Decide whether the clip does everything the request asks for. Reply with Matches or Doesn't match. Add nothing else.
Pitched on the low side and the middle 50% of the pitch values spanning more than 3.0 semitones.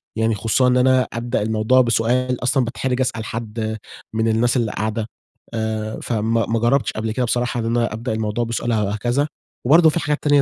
Doesn't match